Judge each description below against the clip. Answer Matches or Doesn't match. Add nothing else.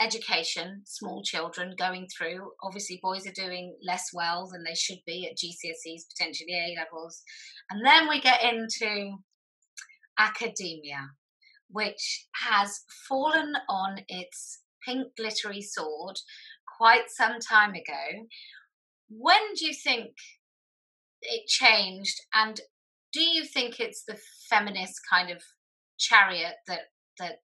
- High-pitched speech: Matches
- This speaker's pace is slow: Matches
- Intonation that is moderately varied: Doesn't match